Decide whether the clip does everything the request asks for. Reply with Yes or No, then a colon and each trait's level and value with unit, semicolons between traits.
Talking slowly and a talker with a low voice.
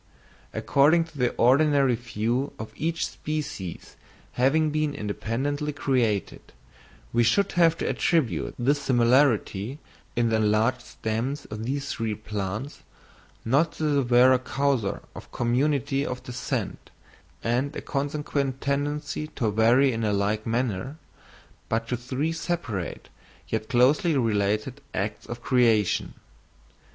Yes: slow, 125 wpm; low, 125 Hz